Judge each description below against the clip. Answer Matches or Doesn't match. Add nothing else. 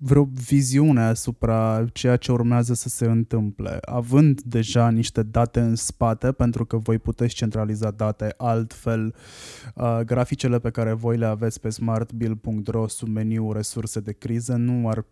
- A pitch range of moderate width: Doesn't match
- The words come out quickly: Doesn't match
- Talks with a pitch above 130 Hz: Doesn't match